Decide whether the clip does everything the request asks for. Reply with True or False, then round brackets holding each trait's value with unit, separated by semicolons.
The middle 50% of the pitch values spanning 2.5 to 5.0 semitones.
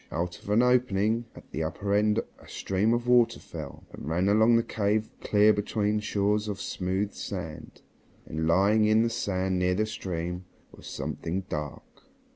True (2.9 semitones)